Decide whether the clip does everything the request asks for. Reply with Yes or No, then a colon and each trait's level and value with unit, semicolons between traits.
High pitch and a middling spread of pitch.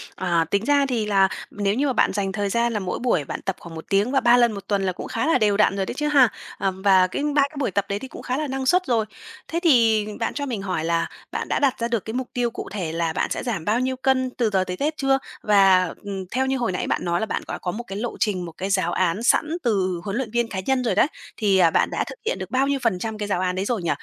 Yes: high, 215 Hz; average, 5.0 semitones